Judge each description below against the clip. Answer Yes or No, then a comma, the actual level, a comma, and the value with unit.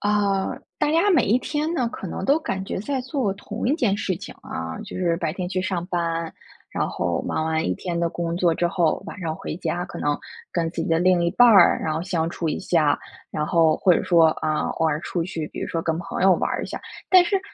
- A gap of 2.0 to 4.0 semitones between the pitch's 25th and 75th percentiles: Yes, average, 3.7 semitones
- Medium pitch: Yes, medium, 175 Hz